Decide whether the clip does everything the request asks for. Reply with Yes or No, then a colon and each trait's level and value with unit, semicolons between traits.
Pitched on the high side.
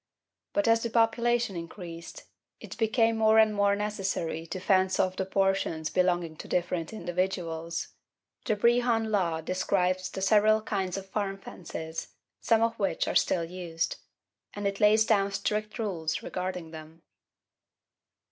Yes: high, 195 Hz